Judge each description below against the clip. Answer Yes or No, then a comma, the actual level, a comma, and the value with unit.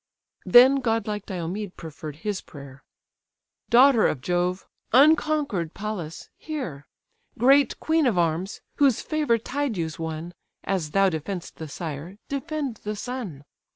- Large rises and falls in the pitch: Yes, wide, 7.9 semitones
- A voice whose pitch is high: Yes, high, 200 Hz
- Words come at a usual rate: No, slow, 120 wpm